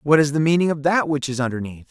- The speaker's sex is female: No, male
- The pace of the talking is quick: Yes, fast, 285 wpm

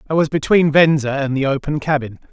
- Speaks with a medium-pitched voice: Yes, medium, 145 Hz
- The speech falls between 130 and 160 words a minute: No, fast, 205 wpm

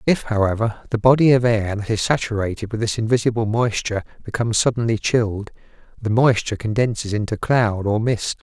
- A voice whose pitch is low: Yes, low, 110 Hz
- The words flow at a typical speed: Yes, average, 160 wpm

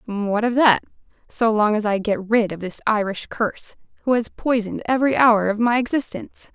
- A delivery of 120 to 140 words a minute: No, average, 195 wpm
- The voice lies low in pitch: No, high, 220 Hz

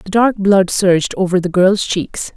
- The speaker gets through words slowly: No, fast, 205 wpm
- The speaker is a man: No, female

